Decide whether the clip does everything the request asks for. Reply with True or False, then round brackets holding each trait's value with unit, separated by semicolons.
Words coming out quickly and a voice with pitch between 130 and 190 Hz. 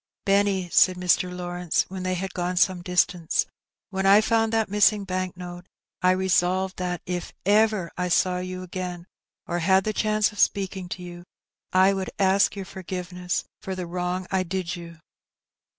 False (170 wpm; 185 Hz)